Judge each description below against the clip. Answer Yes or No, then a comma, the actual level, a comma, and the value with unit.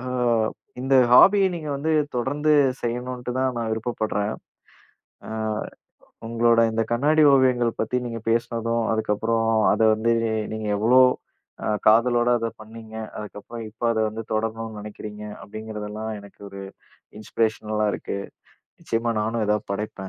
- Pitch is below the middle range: Yes, low, 115 Hz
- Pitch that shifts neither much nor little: No, narrow, 1.9 semitones